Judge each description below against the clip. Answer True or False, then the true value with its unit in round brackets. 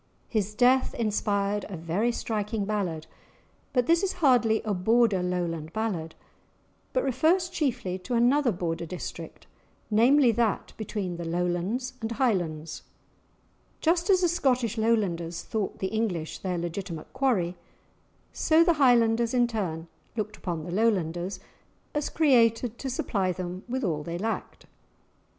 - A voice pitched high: True (215 Hz)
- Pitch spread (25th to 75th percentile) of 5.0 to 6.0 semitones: True (5.6 semitones)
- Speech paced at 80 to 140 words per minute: True (135 wpm)